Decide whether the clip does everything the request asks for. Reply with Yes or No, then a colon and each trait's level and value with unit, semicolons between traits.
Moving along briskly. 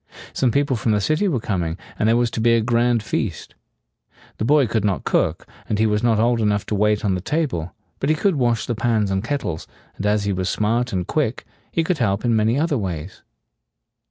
Yes: fast, 225 wpm